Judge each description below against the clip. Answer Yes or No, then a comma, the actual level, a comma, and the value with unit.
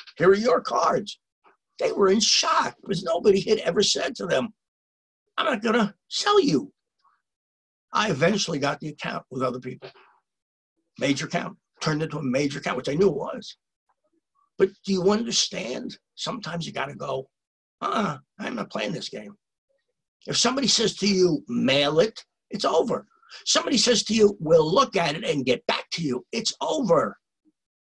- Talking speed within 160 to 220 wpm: Yes, average, 170 wpm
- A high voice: Yes, high, 200 Hz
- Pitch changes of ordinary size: No, wide, 6.3 semitones